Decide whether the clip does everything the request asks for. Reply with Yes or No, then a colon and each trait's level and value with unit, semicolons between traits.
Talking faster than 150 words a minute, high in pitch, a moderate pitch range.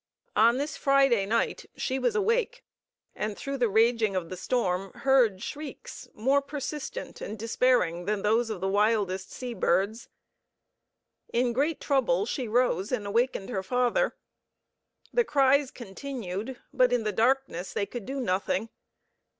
No: average, 145 wpm; high, 235 Hz; average, 4.9 semitones